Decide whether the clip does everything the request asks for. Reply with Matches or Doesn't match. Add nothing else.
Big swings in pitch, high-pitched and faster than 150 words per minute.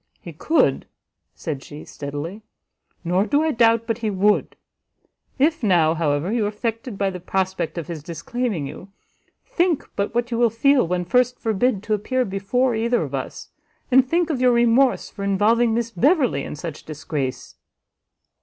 Matches